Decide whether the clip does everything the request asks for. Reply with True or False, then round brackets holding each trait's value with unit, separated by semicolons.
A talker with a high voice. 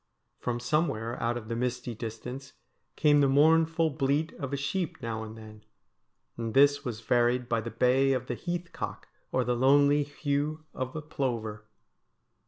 False (130 Hz)